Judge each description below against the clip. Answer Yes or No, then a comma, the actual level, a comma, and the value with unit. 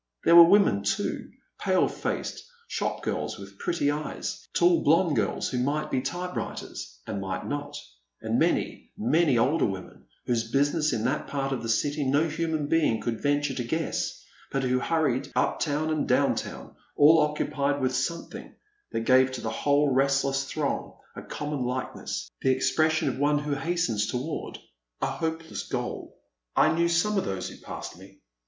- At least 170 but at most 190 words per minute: Yes, average, 175 wpm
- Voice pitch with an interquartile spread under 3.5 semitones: No, average, 3.8 semitones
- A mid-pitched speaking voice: Yes, medium, 145 Hz